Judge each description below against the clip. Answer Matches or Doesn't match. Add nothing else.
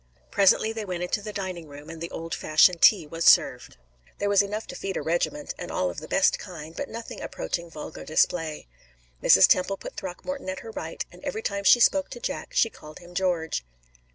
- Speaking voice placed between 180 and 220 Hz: Matches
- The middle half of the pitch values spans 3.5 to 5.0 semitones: Matches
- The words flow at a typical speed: Doesn't match